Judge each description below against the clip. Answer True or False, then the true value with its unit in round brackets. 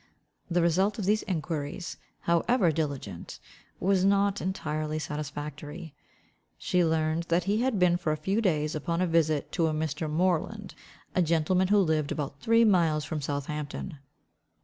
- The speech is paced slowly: False (150 wpm)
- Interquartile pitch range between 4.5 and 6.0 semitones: False (3.6 semitones)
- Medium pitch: True (165 Hz)